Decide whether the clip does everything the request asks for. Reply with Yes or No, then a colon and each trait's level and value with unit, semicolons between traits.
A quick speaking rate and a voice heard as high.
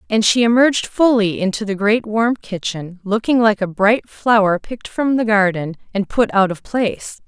No: average, 190 wpm; high, 215 Hz